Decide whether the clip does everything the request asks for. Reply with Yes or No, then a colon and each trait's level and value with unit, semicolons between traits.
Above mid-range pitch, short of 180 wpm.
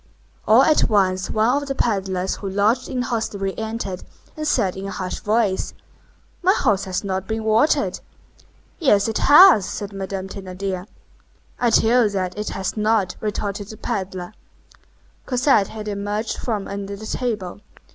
Yes: high, 205 Hz; average, 160 wpm